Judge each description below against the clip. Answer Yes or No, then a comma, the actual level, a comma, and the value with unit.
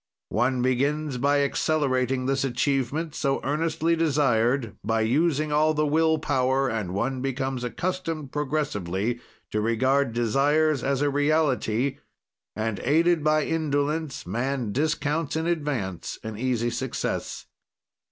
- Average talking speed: No, slow, 125 wpm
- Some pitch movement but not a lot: Yes, average, 3.8 semitones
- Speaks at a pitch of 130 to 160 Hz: Yes, low, 135 Hz